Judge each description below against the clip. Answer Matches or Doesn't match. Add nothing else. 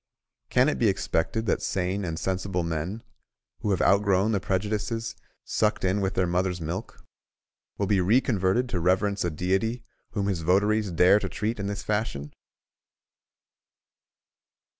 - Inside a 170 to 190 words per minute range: Doesn't match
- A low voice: Matches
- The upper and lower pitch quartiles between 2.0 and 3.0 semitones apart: Matches